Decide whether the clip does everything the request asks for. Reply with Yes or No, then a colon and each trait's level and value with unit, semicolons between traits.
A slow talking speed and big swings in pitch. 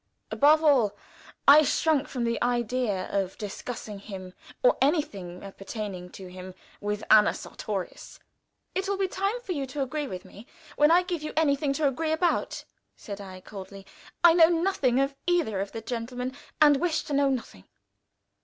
No: average, 170 wpm; wide, 7.2 semitones